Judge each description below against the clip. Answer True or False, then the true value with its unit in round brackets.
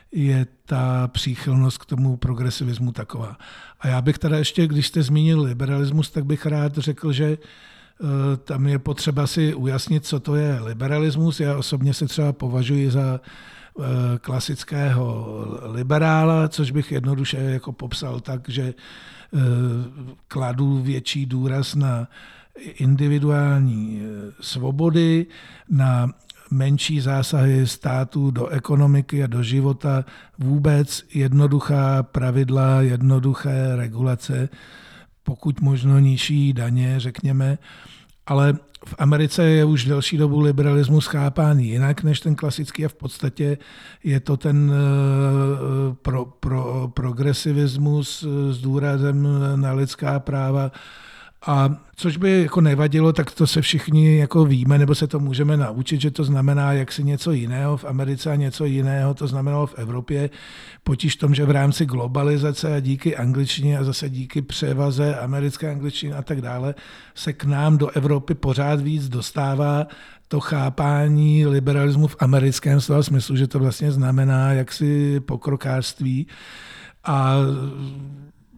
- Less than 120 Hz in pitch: False (140 Hz)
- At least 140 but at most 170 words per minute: False (130 wpm)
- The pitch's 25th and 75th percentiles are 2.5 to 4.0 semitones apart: False (1.9 semitones)